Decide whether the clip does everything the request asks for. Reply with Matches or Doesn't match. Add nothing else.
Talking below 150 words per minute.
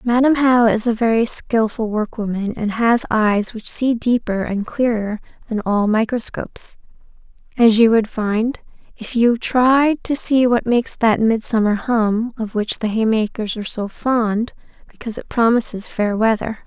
Doesn't match